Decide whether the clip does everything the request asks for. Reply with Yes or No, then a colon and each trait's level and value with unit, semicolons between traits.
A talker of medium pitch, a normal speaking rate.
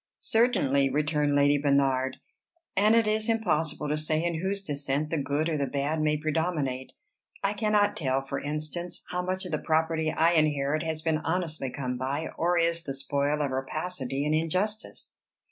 Yes: medium, 155 Hz; average, 175 wpm